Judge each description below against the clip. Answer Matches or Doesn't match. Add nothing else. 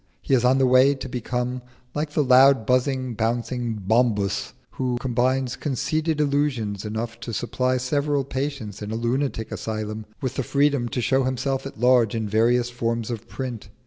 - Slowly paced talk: Doesn't match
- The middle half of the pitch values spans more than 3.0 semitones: Doesn't match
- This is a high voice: Doesn't match